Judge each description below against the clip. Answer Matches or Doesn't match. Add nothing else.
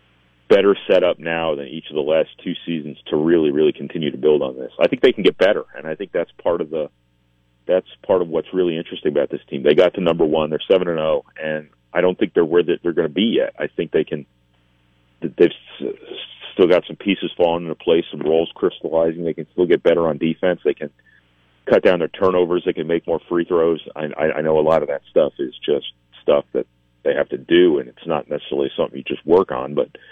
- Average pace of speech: Doesn't match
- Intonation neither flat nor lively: Doesn't match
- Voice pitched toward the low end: Matches